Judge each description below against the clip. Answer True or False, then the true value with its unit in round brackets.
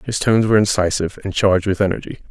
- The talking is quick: True (210 wpm)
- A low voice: True (100 Hz)